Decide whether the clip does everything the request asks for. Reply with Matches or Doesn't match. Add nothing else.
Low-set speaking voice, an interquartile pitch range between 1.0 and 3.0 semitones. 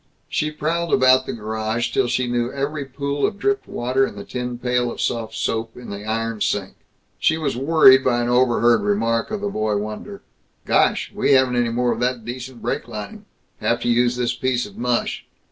Matches